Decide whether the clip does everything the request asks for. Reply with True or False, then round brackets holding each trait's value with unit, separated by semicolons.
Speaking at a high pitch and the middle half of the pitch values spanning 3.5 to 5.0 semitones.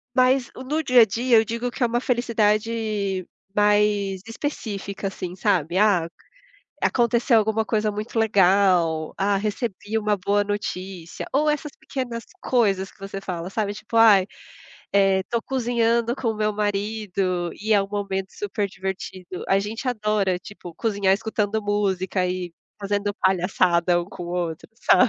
False (205 Hz; 2.9 semitones)